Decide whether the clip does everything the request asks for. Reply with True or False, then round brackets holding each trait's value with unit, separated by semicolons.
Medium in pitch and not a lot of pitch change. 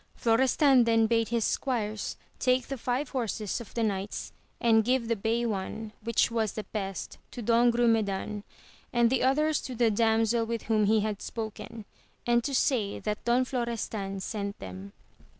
False (225 Hz; 2.2 semitones)